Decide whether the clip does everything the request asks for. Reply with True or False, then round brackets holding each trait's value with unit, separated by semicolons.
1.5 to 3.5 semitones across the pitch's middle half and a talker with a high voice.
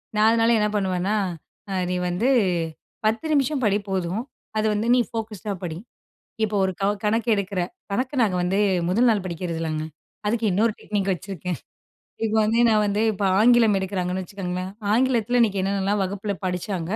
True (3.1 semitones; 205 Hz)